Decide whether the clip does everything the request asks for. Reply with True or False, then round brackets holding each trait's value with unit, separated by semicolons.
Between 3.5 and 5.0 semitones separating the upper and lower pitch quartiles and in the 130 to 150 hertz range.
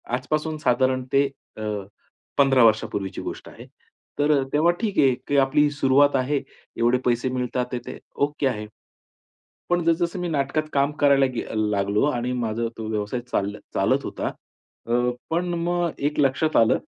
True (3.8 semitones; 135 Hz)